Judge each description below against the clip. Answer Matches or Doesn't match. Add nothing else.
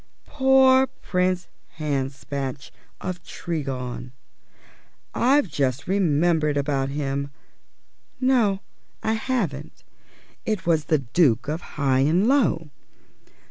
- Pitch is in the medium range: Matches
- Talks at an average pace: Doesn't match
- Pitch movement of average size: Doesn't match